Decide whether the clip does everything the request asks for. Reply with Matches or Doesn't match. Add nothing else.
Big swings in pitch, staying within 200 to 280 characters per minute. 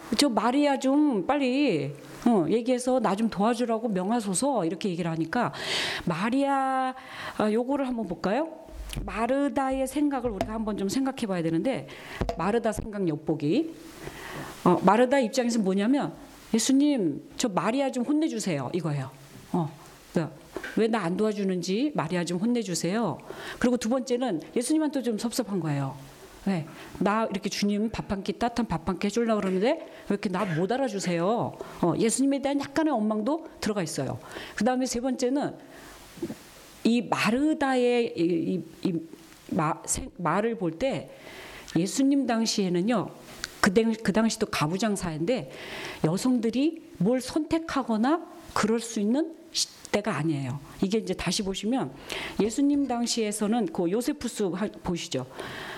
Doesn't match